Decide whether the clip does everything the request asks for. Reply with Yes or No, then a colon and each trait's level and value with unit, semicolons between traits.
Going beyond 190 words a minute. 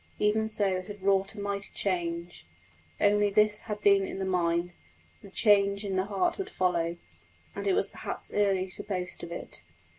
No: average, 185 wpm